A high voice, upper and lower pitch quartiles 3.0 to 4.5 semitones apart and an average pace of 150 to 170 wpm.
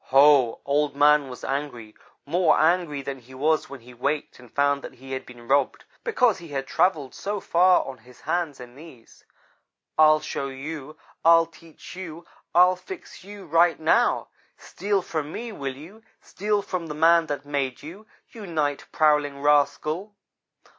No: medium, 150 Hz; average, 3.9 semitones; average, 165 wpm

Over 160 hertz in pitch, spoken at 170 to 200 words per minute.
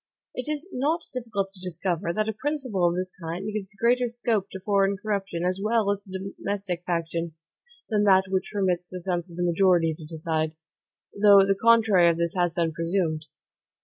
Yes: high, 190 Hz; average, 185 wpm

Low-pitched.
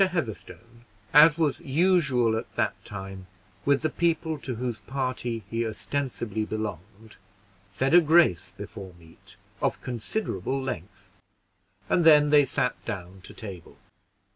Yes: low, 120 Hz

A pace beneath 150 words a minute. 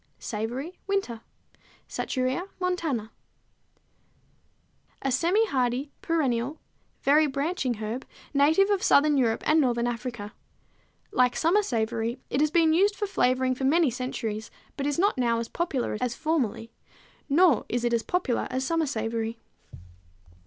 Yes: average, 140 wpm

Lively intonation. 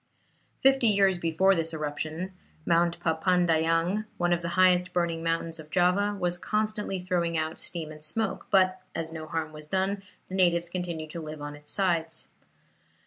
No: narrow, 2.5 semitones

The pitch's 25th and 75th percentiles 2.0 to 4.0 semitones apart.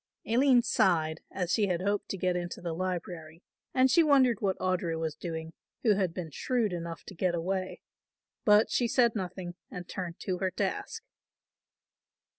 Yes: average, 3.7 semitones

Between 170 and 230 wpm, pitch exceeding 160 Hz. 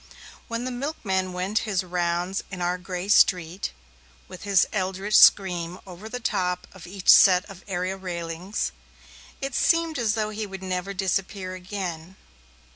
No: average, 150 wpm; high, 190 Hz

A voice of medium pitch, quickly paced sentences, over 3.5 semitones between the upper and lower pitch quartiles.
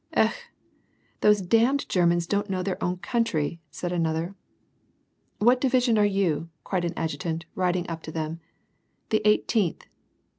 No: medium, 180 Hz; average, 160 wpm; average, 4.2 semitones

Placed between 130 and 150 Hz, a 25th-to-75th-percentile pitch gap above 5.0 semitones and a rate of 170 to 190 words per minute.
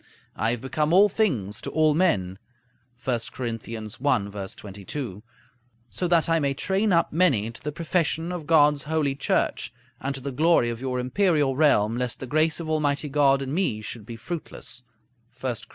Yes: medium, 140 Hz; wide, 5.4 semitones; average, 180 wpm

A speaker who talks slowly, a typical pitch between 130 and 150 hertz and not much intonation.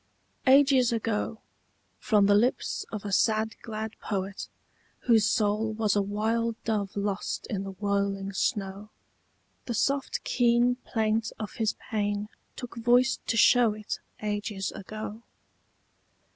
No: slow, 130 wpm; high, 215 Hz; narrow, 2.2 semitones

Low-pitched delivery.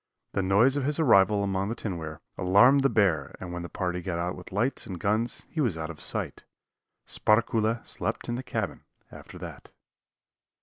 Yes: low, 100 Hz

